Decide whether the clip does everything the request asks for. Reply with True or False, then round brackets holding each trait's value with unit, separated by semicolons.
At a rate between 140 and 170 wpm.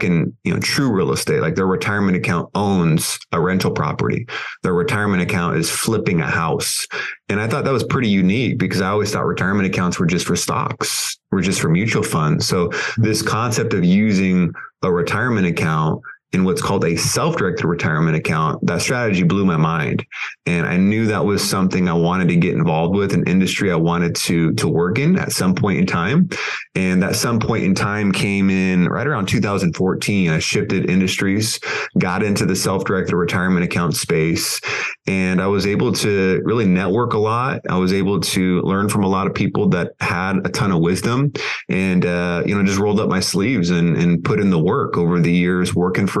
False (200 wpm)